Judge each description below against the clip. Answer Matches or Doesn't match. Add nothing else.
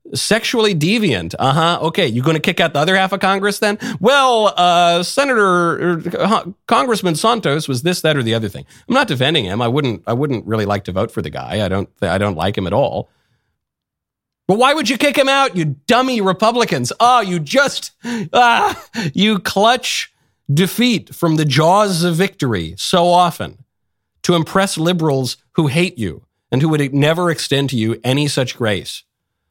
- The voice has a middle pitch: Matches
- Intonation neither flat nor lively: Doesn't match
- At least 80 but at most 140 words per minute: Doesn't match